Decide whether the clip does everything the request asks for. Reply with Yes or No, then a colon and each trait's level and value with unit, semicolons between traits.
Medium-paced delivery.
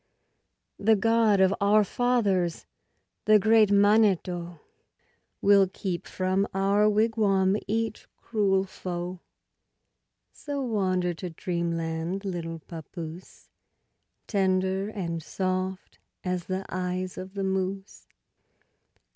No: slow, 95 wpm